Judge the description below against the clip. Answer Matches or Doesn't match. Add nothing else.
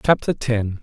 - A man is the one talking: Matches